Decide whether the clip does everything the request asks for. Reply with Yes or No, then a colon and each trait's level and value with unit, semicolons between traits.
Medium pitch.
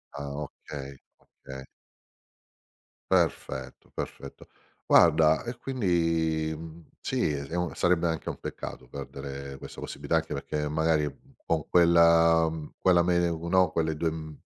No: very low, 80 Hz